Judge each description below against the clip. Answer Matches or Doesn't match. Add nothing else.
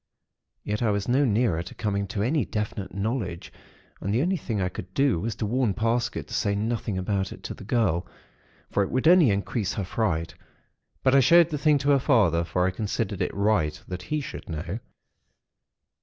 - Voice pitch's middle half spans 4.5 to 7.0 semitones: Matches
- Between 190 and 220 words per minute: Matches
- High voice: Doesn't match